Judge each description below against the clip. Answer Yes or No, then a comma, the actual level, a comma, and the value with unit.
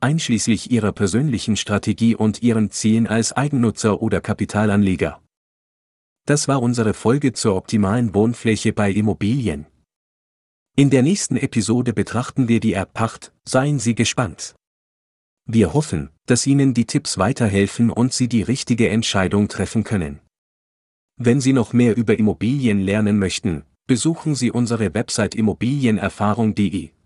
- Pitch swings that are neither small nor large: Yes, average, 3.1 semitones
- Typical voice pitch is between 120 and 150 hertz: No, low, 110 Hz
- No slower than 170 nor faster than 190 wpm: No, average, 130 wpm